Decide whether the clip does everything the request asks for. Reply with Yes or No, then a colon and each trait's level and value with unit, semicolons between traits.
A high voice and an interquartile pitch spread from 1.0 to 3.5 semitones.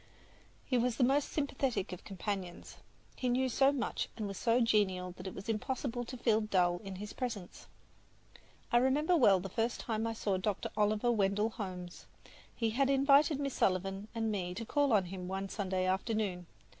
No: high, 215 Hz; average, 4.6 semitones